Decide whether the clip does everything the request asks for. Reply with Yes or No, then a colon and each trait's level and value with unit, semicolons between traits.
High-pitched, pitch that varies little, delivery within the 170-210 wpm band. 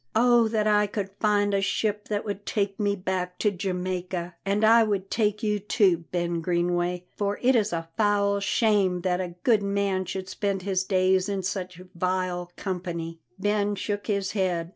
Yes: high, 195 Hz; narrow, 2.3 semitones; average, 180 wpm